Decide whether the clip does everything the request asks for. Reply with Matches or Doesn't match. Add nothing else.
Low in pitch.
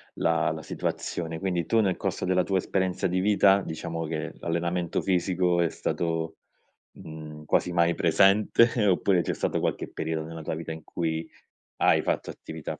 Matches